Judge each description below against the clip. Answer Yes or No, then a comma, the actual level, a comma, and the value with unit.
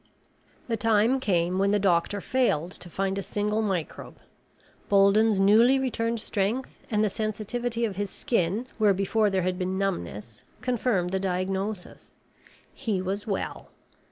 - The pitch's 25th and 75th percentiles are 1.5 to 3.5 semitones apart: Yes, average, 2.9 semitones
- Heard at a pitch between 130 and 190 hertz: No, high, 200 Hz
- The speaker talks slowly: No, average, 145 wpm